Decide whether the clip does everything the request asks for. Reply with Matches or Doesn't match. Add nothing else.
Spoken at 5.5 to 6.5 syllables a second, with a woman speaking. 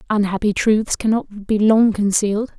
Doesn't match